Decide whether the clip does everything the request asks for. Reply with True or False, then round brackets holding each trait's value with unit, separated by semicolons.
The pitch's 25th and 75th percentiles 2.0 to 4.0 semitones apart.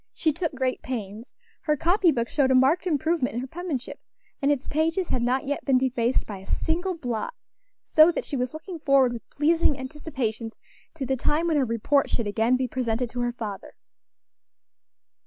False (4.5 semitones)